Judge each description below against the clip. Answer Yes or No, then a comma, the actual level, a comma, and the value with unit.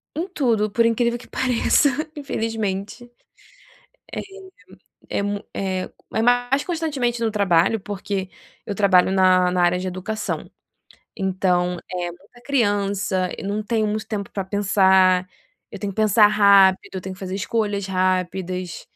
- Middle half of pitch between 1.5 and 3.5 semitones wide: Yes, average, 3.2 semitones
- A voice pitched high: Yes, high, 200 Hz